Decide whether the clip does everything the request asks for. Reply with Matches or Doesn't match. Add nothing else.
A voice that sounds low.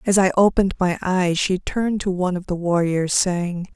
Doesn't match